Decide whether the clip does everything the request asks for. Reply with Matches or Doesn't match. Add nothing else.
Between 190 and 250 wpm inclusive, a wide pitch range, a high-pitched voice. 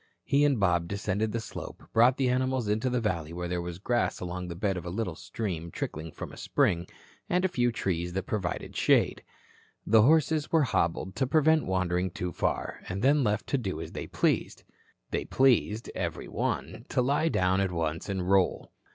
Doesn't match